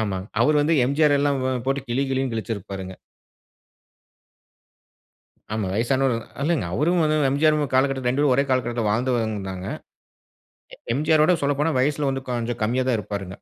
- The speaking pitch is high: No, low, 130 Hz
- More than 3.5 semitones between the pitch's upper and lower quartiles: Yes, average, 4.2 semitones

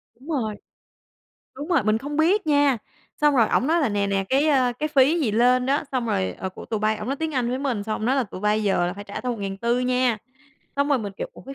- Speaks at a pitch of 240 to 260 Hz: Yes, very high, 250 Hz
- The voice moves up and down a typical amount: Yes, average, 4.9 semitones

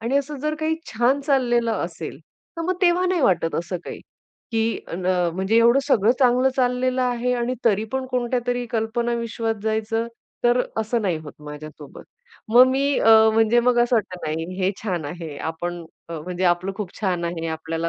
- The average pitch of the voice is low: No, high, 225 Hz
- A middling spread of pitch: No, wide, 5.8 semitones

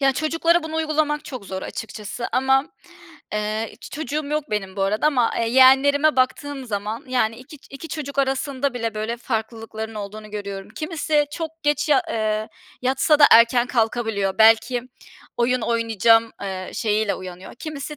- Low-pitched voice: No, high, 245 Hz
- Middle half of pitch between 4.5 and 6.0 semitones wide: Yes, average, 4.8 semitones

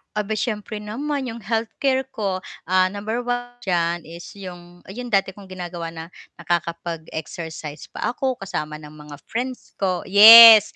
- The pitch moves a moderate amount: Yes, average, 5.0 semitones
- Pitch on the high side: Yes, high, 195 Hz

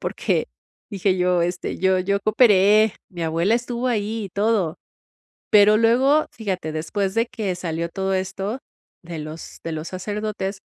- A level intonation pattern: No, average, 3.2 semitones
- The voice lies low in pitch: No, high, 195 Hz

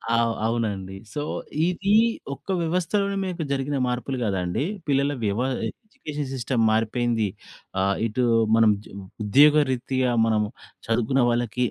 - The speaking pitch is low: Yes, low, 125 Hz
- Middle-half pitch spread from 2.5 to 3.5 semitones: No, average, 4.4 semitones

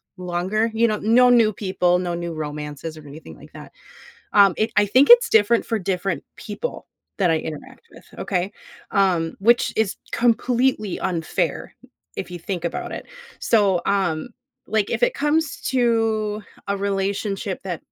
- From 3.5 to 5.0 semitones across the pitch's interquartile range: Yes, average, 4.3 semitones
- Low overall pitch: No, high, 200 Hz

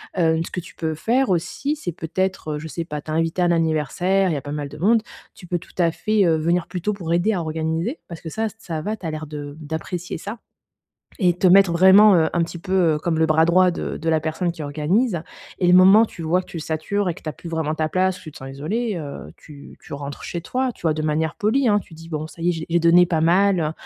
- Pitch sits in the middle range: Yes, medium, 170 Hz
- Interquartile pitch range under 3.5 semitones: Yes, average, 2.9 semitones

